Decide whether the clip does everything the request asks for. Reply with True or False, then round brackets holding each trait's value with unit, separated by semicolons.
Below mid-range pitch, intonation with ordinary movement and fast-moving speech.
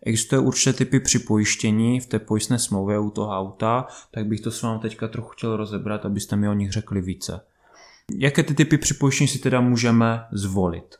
True (110 Hz; 3.4 semitones; 185 wpm)